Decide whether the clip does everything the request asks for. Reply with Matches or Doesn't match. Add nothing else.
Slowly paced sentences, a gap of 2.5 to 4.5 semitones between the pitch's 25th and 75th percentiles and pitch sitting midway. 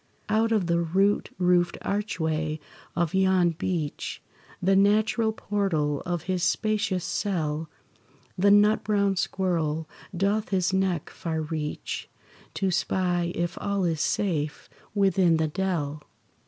Matches